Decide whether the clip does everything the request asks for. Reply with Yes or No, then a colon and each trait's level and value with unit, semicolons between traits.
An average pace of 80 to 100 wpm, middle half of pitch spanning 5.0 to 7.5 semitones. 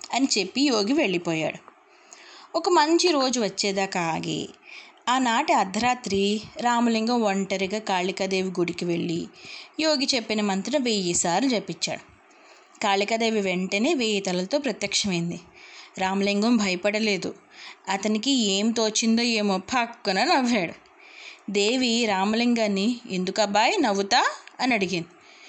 Yes: average, 95 wpm; average, 5.3 semitones